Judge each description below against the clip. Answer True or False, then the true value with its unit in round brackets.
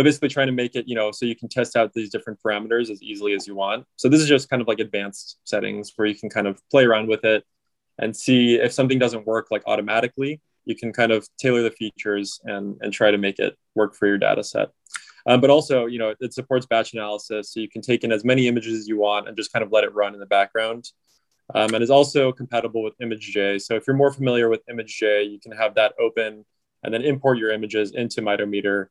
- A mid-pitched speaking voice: False (115 Hz)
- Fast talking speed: True (250 wpm)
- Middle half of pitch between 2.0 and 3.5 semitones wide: True (2.7 semitones)